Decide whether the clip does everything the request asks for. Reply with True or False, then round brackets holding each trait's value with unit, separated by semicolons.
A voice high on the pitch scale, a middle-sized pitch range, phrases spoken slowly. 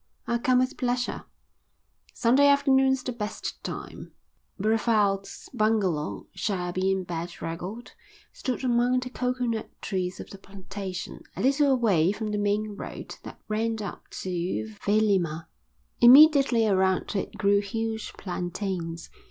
True (210 Hz; 4.5 semitones; 125 wpm)